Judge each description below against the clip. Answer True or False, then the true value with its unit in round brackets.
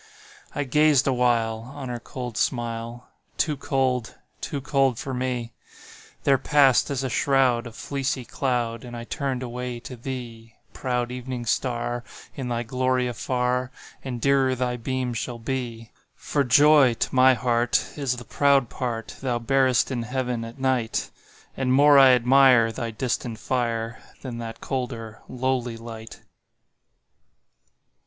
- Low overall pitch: True (125 Hz)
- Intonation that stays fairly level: True (2.0 semitones)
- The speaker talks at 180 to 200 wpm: False (140 wpm)